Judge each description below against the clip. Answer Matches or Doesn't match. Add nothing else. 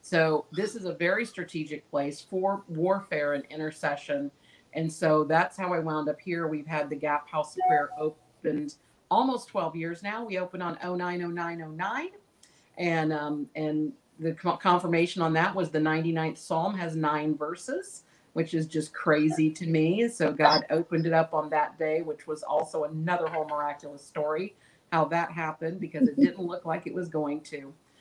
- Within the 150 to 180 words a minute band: Matches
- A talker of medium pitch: Matches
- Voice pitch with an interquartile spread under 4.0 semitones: Matches